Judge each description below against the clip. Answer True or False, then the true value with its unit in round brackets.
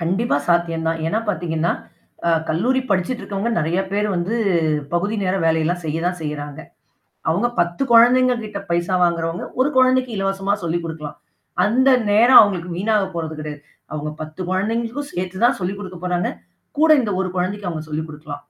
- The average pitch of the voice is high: False (180 Hz)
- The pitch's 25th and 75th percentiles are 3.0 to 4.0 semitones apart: False (4.4 semitones)